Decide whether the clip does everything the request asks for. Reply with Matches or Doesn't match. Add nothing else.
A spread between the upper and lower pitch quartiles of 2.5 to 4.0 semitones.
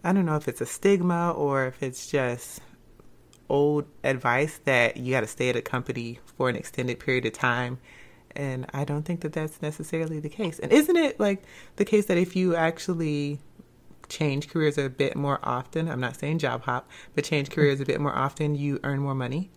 Matches